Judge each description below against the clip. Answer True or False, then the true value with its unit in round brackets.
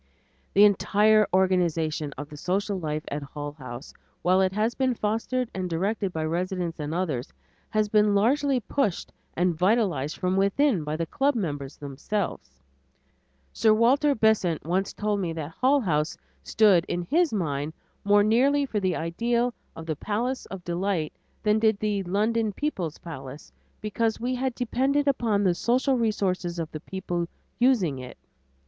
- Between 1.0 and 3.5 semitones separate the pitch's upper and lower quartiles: False (5.5 semitones)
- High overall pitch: True (195 Hz)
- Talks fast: False (160 wpm)